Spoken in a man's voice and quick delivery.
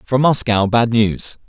No: male; average, 160 wpm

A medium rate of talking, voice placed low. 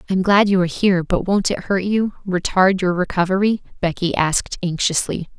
No: average, 190 wpm; medium, 185 Hz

